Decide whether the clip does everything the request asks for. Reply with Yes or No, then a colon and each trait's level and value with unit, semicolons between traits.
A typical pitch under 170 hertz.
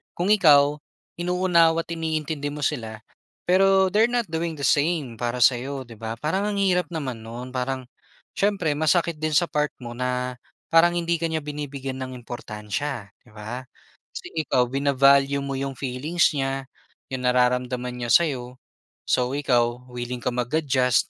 Yes: medium, 140 Hz